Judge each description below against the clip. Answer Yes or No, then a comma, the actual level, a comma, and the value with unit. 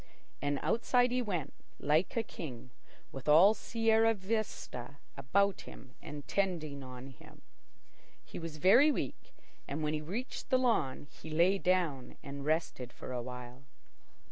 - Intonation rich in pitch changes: Yes, wide, 6.7 semitones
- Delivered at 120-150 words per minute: Yes, average, 145 wpm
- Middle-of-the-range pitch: Yes, medium, 155 Hz